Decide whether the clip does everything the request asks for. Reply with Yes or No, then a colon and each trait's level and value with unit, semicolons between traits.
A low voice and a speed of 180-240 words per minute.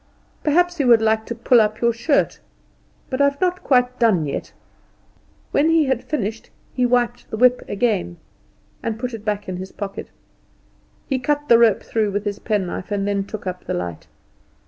No: high, 230 Hz; average, 185 wpm